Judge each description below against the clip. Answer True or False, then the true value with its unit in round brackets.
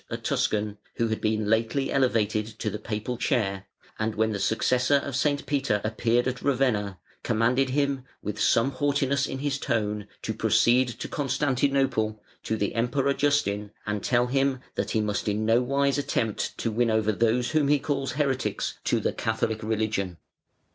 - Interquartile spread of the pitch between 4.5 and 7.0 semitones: False (4.0 semitones)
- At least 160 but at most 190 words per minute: True (170 wpm)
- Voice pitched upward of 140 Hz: False (120 Hz)